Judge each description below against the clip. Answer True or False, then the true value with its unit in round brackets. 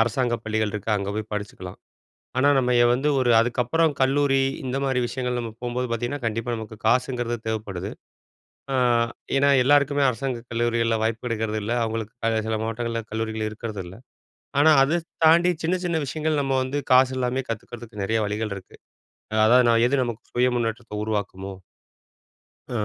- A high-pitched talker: False (120 Hz)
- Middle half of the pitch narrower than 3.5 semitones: True (3.0 semitones)